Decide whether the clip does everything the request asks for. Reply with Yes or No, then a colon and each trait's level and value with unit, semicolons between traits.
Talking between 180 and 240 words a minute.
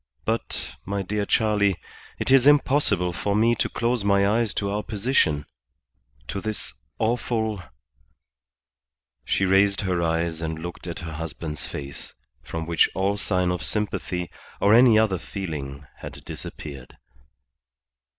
No: average, 140 wpm